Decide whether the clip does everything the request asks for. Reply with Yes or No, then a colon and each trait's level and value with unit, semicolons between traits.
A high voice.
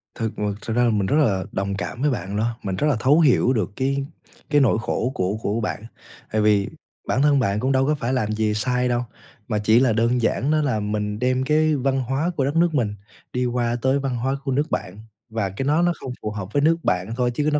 No: low, 125 Hz